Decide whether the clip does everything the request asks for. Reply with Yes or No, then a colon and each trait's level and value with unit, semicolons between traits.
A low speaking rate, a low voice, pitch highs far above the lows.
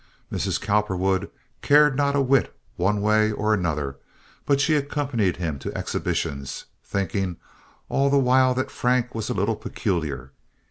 No: average, 145 wpm; low, 105 Hz; wide, 6.4 semitones